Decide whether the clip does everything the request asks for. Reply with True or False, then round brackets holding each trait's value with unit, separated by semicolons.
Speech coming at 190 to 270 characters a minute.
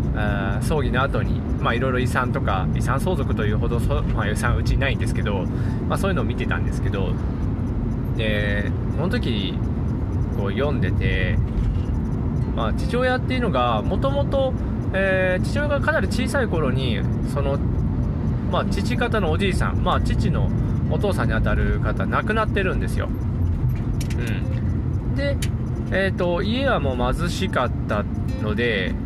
False (295 characters per minute)